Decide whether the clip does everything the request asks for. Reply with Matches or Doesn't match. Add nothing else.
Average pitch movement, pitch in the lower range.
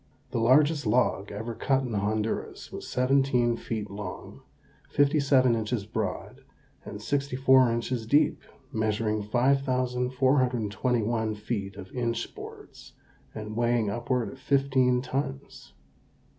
Matches